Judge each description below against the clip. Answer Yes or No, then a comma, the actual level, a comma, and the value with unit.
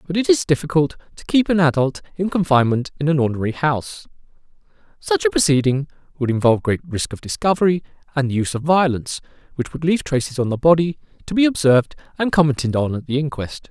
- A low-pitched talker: No, medium, 150 Hz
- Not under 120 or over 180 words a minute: No, average, 195 wpm